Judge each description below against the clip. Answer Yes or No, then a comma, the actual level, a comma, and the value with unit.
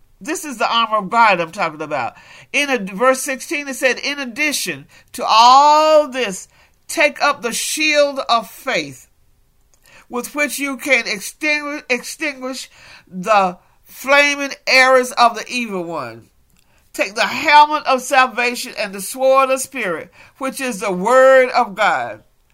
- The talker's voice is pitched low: No, very high, 260 Hz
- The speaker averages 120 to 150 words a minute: Yes, average, 140 wpm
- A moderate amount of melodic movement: Yes, average, 3.6 semitones